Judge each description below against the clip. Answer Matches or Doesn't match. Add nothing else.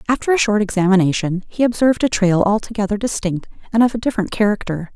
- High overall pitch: Matches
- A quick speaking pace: Doesn't match